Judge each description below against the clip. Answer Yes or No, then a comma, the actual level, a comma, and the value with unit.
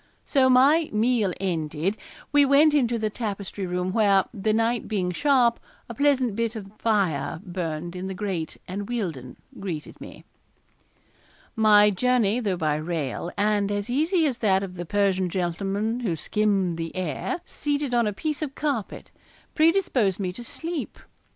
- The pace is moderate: Yes, average, 155 wpm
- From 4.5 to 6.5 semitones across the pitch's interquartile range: Yes, average, 5.0 semitones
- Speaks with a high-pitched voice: Yes, high, 205 Hz